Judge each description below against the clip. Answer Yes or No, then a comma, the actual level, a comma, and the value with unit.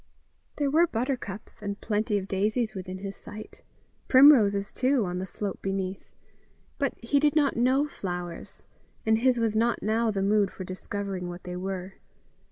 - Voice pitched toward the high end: Yes, high, 210 Hz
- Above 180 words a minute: No, average, 165 wpm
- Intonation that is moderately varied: Yes, average, 4.3 semitones